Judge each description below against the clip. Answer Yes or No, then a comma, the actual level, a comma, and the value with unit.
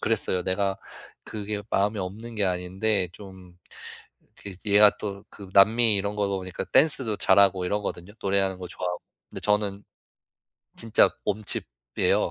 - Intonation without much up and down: Yes, narrow, 2.0 semitones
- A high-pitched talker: No, low, 100 Hz